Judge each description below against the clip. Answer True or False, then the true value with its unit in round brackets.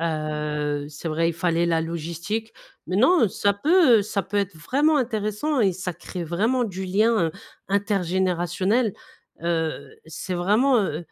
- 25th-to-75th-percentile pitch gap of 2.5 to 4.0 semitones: False (4.5 semitones)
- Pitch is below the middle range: False (185 Hz)